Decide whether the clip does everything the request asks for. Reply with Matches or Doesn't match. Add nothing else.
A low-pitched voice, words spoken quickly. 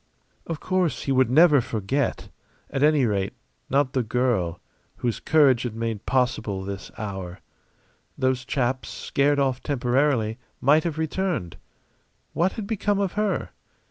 Doesn't match